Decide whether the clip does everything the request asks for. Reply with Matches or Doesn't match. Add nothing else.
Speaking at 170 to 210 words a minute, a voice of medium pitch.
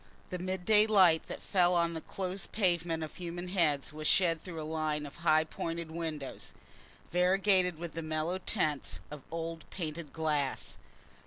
Doesn't match